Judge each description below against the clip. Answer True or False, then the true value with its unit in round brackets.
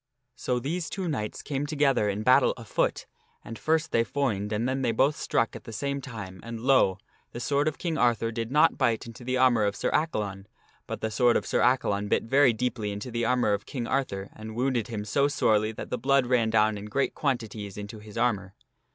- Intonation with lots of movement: False (4.1 semitones)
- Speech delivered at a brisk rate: True (220 wpm)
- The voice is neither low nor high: False (115 Hz)